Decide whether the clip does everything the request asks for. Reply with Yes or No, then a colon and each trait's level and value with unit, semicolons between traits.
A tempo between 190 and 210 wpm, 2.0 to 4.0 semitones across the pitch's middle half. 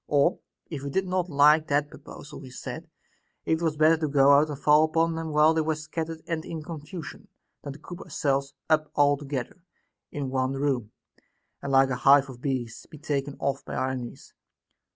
Yes: average, 195 wpm; narrow, 2.5 semitones